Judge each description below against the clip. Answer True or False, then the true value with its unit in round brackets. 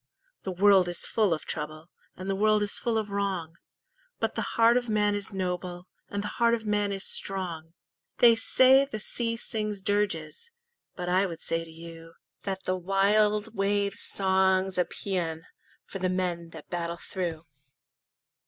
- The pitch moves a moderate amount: True (3.1 semitones)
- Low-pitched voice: False (195 Hz)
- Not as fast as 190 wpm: True (170 wpm)